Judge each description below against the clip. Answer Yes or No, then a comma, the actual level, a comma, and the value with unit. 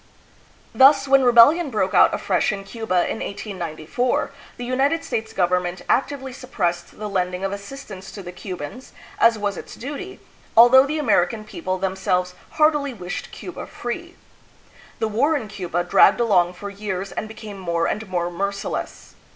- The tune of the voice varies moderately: No, wide, 5.7 semitones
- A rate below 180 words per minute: Yes, average, 160 wpm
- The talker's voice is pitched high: Yes, high, 210 Hz